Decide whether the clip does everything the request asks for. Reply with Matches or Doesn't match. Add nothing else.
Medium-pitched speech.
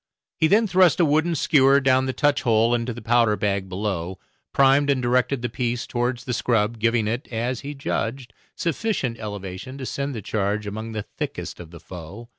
Doesn't match